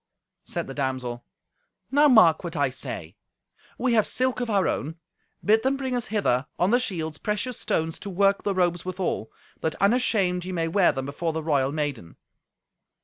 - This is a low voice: No, medium, 180 Hz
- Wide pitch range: Yes, wide, 6.2 semitones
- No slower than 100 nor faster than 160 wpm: No, average, 180 wpm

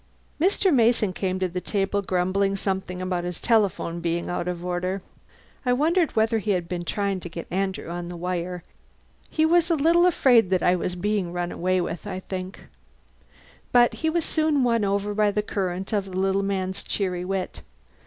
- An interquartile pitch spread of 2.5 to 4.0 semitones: Yes, average, 3.5 semitones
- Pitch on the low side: No, high, 190 Hz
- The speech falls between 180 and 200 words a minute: Yes, average, 190 wpm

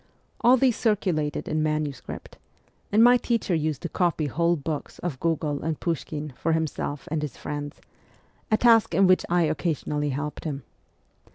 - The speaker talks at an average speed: Yes, average, 170 wpm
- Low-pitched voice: No, medium, 160 Hz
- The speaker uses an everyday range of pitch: Yes, average, 3.5 semitones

